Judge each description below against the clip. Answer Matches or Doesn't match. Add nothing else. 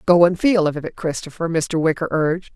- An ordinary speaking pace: Doesn't match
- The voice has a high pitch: Doesn't match